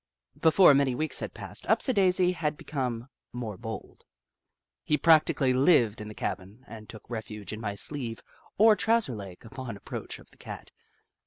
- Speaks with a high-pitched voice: No, low, 125 Hz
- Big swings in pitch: Yes, wide, 6.3 semitones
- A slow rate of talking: No, average, 160 wpm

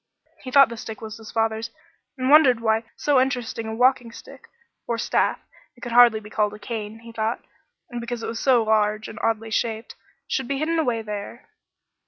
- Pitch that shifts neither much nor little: No, narrow, 2.1 semitones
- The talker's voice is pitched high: Yes, high, 230 Hz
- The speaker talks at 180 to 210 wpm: Yes, average, 195 wpm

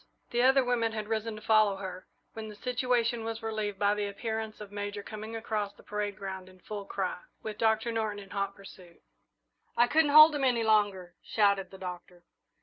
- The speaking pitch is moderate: No, high, 215 Hz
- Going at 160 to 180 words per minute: No, average, 195 wpm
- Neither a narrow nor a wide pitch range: No, narrow, 2.3 semitones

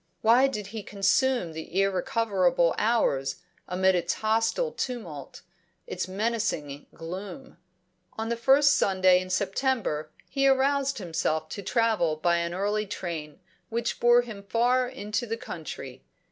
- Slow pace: Yes, slow, 130 wpm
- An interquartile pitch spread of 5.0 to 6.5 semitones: Yes, wide, 5.4 semitones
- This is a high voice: Yes, high, 205 Hz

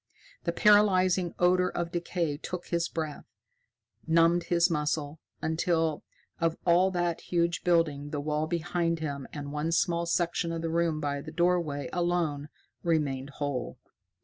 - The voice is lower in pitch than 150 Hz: No, medium, 165 Hz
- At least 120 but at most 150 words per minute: Yes, average, 145 wpm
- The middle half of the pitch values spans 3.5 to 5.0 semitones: No, narrow, 2.5 semitones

